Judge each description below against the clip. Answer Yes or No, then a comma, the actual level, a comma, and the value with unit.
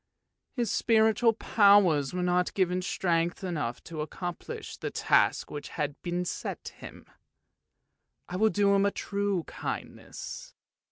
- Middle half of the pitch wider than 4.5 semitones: No, average, 3.1 semitones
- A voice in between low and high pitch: Yes, medium, 180 Hz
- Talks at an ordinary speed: No, slow, 130 wpm